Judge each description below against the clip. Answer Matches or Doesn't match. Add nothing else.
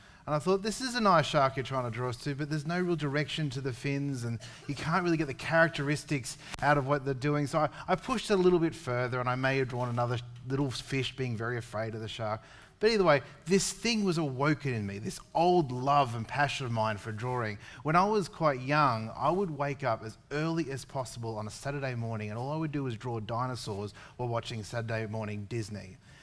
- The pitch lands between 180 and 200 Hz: Doesn't match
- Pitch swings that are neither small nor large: Matches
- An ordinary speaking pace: Doesn't match